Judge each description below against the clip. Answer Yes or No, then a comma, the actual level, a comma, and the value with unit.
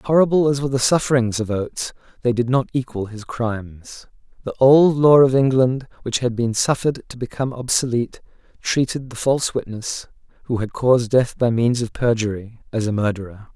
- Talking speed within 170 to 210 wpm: Yes, average, 175 wpm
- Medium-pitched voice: No, low, 120 Hz